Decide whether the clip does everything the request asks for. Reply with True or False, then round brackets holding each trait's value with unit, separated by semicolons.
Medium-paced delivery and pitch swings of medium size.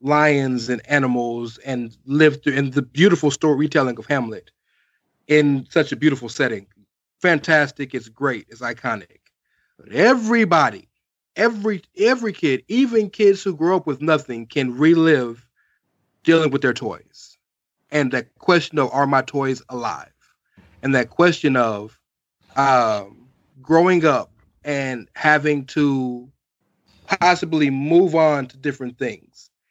False (125 wpm; 4.0 semitones)